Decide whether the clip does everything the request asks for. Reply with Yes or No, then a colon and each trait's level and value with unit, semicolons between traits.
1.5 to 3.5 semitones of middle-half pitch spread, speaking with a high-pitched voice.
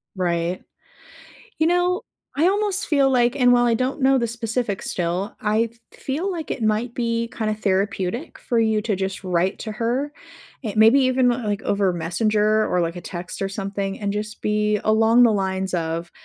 No: average, 4.1 semitones; high, 215 Hz